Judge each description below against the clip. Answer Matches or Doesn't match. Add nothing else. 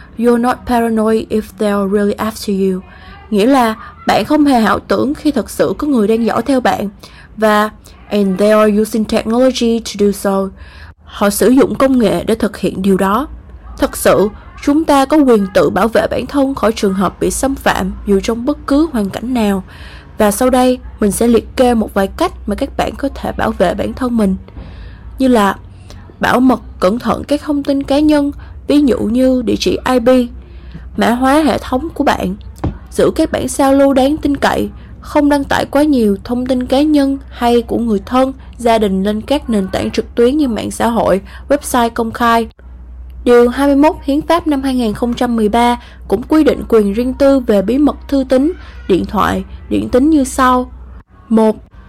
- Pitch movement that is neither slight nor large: Matches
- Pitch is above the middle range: Matches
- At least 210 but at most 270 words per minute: Doesn't match